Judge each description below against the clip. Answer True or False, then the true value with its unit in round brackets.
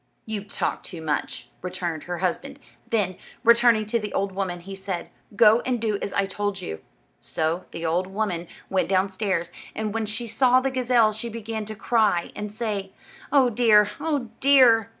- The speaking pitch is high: True (210 Hz)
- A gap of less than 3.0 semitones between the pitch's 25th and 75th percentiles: False (3.5 semitones)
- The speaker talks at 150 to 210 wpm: True (175 wpm)